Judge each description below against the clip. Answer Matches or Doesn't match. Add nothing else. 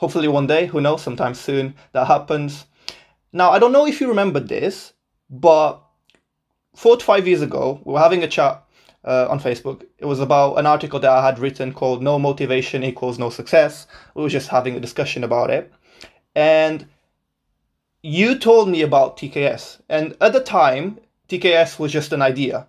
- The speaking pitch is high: Doesn't match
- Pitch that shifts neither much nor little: Matches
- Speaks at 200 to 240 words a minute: Doesn't match